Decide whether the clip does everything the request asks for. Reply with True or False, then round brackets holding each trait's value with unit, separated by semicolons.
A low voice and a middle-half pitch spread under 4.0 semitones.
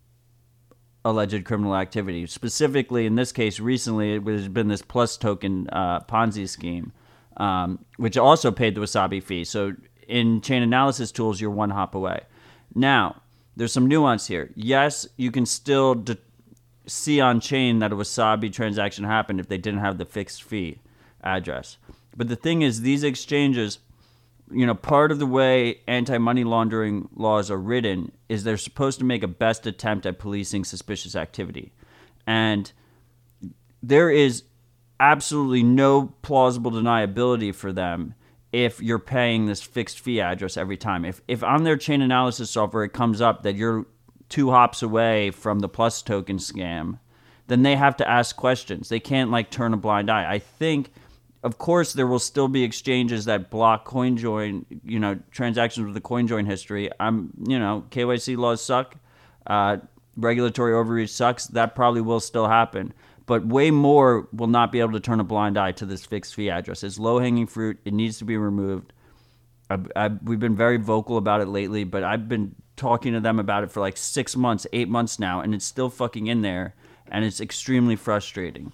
True (115 Hz; 2.8 semitones)